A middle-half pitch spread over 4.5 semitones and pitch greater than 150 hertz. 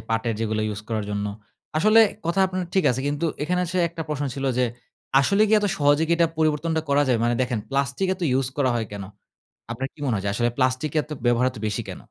No: wide, 5.5 semitones; medium, 140 Hz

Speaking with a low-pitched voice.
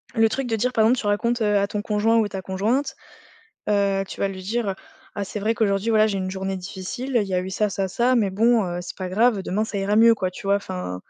No: high, 205 Hz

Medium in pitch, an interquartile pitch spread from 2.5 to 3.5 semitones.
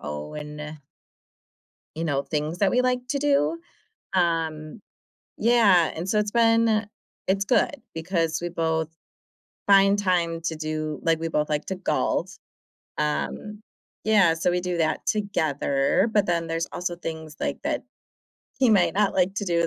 No: medium, 170 Hz; average, 4.3 semitones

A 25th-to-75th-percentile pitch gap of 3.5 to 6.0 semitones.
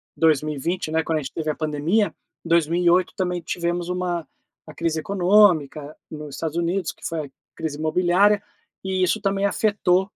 No: average, 2.9 semitones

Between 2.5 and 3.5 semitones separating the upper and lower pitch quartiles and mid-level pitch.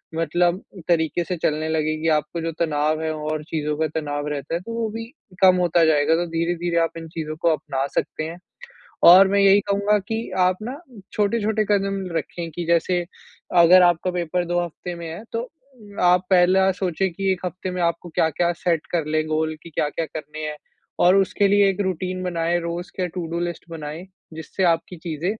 Yes: average, 2.9 semitones; medium, 175 Hz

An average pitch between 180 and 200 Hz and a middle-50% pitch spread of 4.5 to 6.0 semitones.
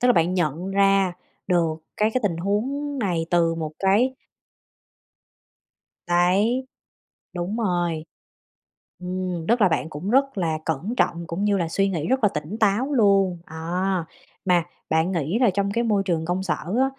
No: medium, 185 Hz; average, 3.8 semitones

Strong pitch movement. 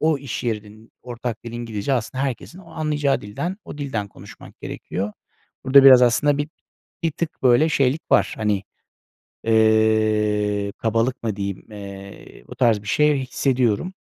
No: average, 4.6 semitones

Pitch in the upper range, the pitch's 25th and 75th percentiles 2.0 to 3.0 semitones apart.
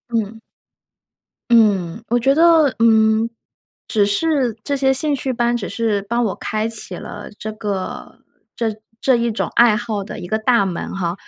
Yes: high, 225 Hz; average, 2.7 semitones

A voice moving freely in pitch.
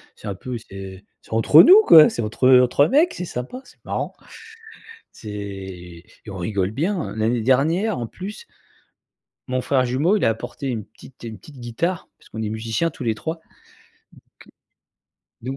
Yes: wide, 6.5 semitones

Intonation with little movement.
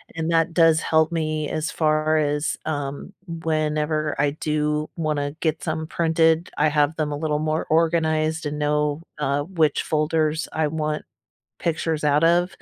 Yes: narrow, 1.3 semitones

